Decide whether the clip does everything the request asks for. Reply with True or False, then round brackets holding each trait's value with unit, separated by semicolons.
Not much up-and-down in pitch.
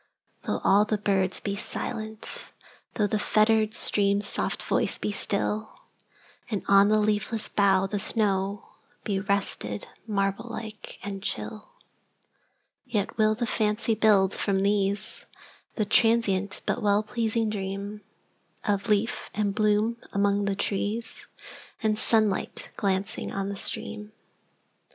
True (1.5 semitones)